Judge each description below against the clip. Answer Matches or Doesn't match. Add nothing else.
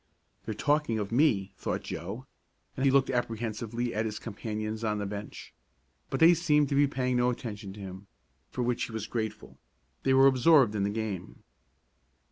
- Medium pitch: Doesn't match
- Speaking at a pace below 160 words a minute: Doesn't match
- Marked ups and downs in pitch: Doesn't match